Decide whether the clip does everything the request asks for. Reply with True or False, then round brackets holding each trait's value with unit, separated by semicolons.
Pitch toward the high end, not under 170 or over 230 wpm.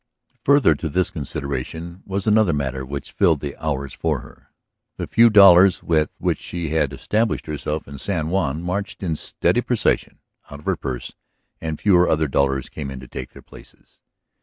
False (80 Hz; 175 wpm)